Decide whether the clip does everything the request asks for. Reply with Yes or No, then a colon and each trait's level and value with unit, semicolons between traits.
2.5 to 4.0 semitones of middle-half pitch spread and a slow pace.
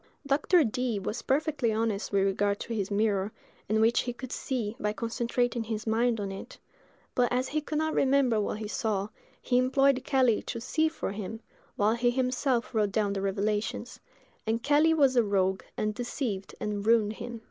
No: average, 3.5 semitones; average, 185 wpm